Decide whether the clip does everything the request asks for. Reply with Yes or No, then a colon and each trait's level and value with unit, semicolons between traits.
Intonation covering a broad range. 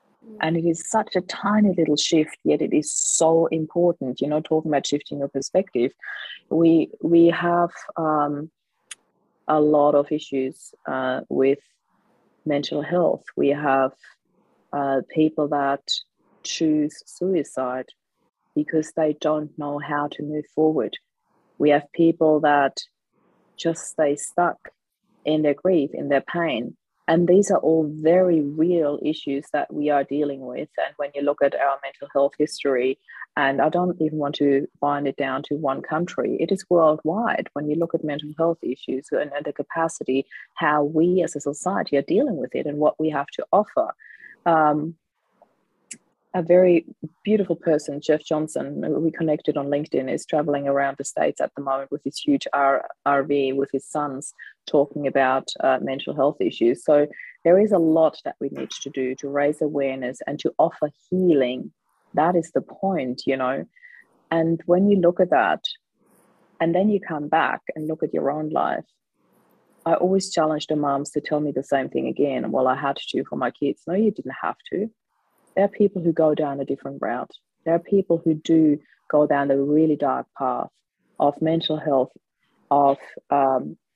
No: average, 2.7 semitones